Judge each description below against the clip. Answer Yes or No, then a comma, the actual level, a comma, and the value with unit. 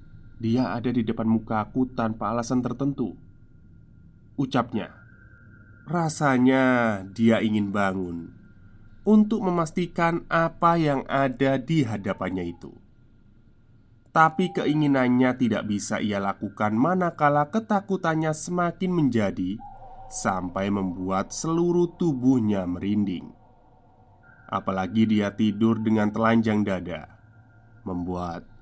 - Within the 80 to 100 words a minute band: Yes, average, 90 wpm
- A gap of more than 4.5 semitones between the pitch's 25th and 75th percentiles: Yes, average, 5.1 semitones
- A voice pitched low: Yes, low, 115 Hz